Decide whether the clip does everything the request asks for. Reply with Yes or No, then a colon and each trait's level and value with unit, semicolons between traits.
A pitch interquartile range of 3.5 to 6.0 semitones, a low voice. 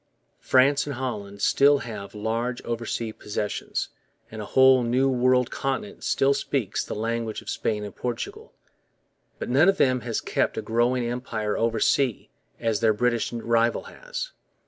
No: average, 2.8 semitones; low, 120 Hz